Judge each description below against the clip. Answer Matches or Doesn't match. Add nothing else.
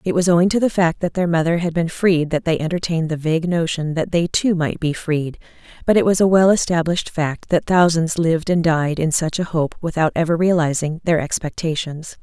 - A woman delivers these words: Matches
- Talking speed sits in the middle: Doesn't match